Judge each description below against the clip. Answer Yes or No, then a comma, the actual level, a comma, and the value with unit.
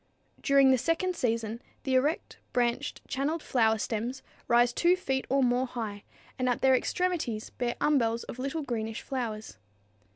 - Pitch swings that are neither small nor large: Yes, average, 3.1 semitones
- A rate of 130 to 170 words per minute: Yes, average, 155 wpm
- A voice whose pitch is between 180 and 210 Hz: No, very high, 255 Hz